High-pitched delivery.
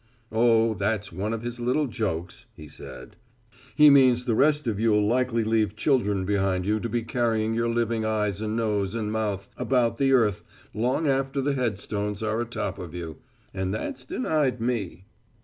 No: low, 110 Hz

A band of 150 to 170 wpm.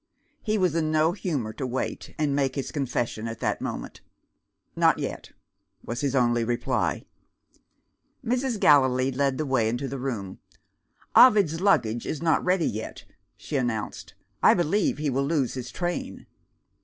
Yes: average, 155 wpm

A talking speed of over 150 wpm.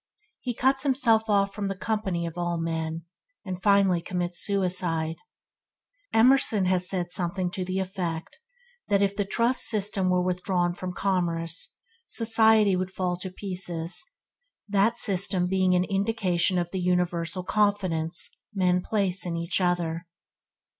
No: average, 140 wpm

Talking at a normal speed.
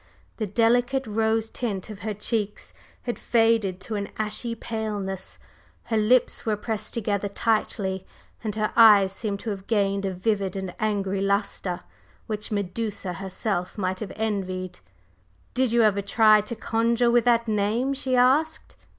Yes: average, 150 wpm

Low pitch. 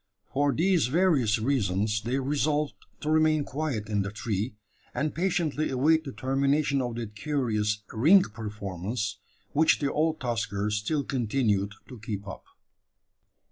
Yes: low, 130 Hz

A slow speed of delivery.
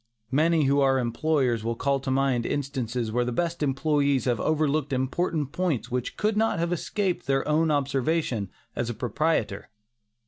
No: average, 165 wpm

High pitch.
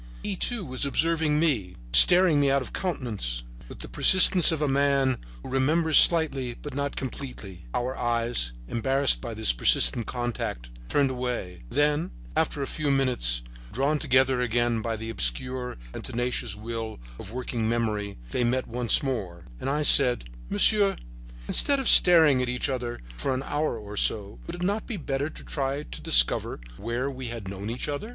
No: low, 130 Hz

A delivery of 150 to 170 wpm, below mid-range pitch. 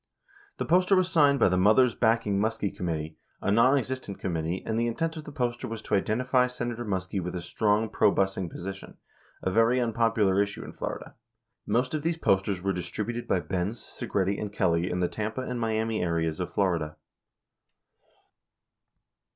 Yes: average, 165 wpm; low, 105 Hz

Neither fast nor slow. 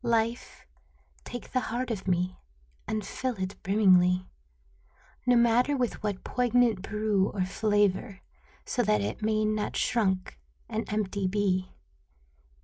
No: slow, 130 wpm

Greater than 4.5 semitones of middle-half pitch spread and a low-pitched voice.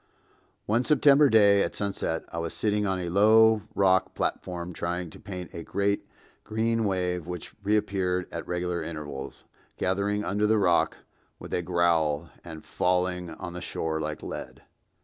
No: average, 3.0 semitones; very low, 90 Hz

